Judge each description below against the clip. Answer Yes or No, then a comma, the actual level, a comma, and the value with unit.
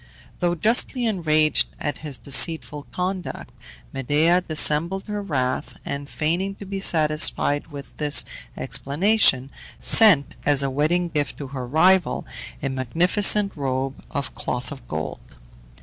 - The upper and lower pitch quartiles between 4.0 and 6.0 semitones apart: Yes, average, 4.7 semitones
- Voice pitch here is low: No, medium, 155 Hz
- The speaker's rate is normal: No, slow, 130 wpm